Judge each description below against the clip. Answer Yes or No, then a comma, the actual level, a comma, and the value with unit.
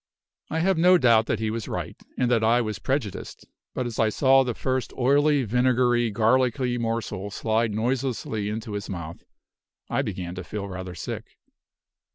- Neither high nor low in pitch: No, low, 115 Hz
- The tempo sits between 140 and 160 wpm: No, average, 170 wpm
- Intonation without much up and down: No, average, 3.3 semitones